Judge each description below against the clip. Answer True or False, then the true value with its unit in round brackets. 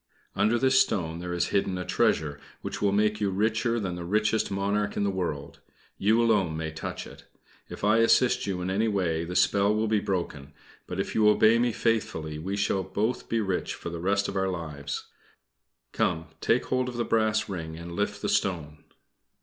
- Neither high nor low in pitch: False (100 Hz)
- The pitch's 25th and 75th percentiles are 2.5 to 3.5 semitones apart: False (4.0 semitones)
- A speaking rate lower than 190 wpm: False (200 wpm)